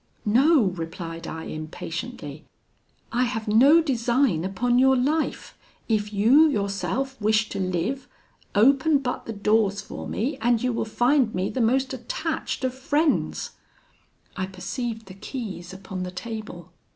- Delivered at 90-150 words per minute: Yes, average, 140 wpm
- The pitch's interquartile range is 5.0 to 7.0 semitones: Yes, wide, 5.6 semitones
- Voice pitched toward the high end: Yes, high, 225 Hz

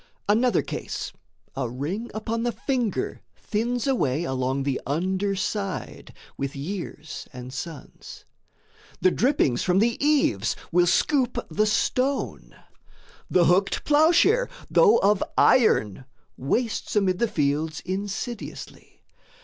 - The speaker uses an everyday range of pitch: No, wide, 8.1 semitones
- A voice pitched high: Yes, high, 195 Hz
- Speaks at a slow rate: Yes, slow, 115 wpm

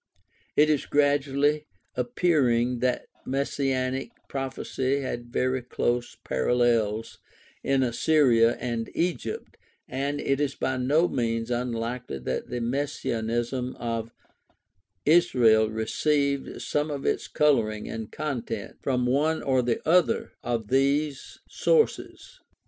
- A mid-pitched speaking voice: No, low, 130 Hz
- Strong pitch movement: No, average, 3.3 semitones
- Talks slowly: Yes, slow, 110 wpm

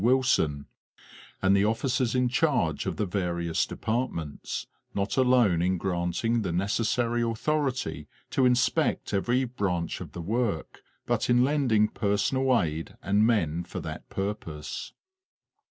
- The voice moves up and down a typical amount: No, wide, 6.0 semitones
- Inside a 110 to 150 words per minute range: Yes, slow, 135 wpm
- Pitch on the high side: No, low, 105 Hz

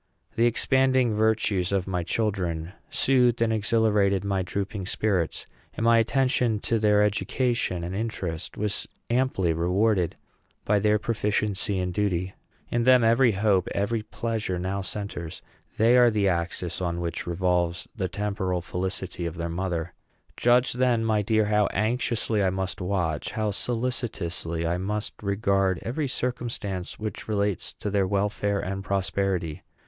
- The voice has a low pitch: Yes, low, 100 Hz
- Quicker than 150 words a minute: No, average, 145 wpm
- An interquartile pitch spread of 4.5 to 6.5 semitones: No, average, 3.6 semitones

